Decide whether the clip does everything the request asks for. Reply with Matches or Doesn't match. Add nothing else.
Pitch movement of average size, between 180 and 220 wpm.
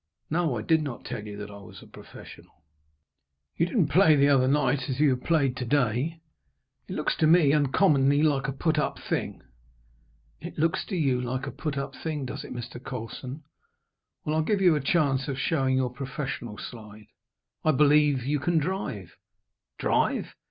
Matches